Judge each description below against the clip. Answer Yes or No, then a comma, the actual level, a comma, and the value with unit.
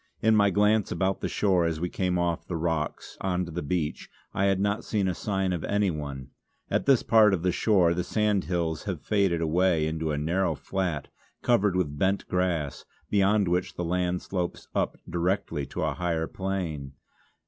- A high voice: No, very low, 90 Hz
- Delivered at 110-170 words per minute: No, average, 185 wpm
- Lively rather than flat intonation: No, average, 2.9 semitones